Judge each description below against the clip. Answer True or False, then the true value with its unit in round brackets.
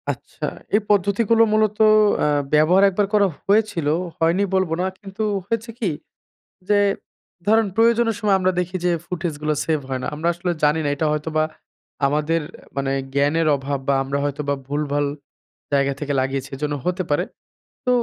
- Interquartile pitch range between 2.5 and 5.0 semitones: False (5.6 semitones)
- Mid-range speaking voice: True (165 Hz)